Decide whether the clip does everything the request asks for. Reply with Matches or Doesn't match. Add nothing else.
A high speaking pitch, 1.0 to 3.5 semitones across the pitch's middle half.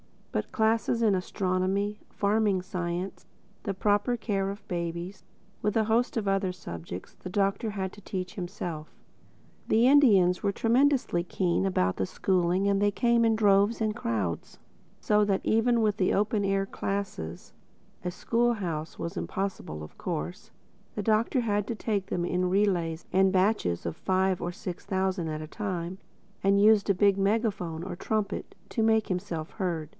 Matches